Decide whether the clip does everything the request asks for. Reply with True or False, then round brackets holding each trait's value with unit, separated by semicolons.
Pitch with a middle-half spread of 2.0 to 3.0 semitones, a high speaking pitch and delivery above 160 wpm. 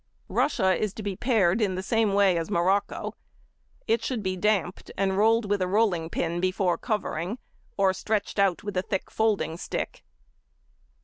True (2.7 semitones; 195 Hz; 170 wpm)